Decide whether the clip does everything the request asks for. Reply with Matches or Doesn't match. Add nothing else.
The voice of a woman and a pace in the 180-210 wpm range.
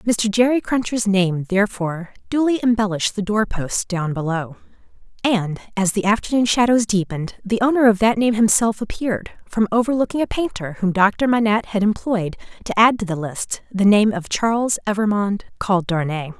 Doesn't match